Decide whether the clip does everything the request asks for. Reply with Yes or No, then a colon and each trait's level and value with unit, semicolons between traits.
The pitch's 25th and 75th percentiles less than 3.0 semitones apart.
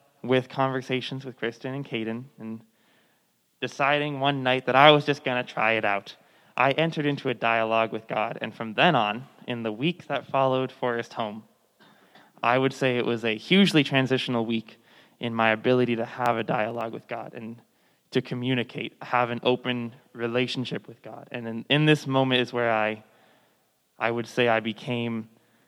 Yes: narrow, 2.6 semitones